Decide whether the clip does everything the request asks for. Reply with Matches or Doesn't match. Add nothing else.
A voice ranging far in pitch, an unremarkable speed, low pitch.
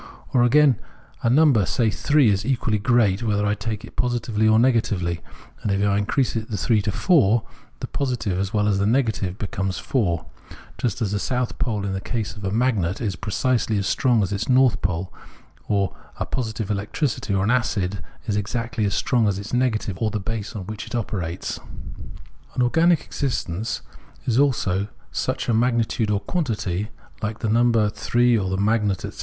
Doesn't match